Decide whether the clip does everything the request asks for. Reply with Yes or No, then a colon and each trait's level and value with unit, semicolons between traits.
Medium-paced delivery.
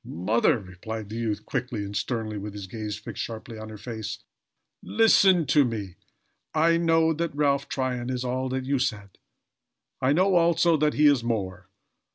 Yes: average, 175 wpm